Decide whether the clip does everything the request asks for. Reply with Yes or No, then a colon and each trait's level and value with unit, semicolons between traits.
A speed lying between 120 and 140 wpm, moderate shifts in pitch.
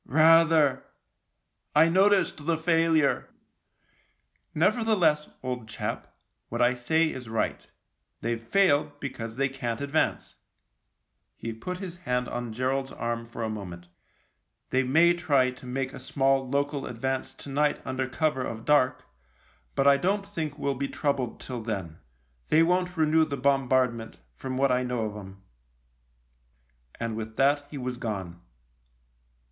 No: average, 150 wpm; average, 4.3 semitones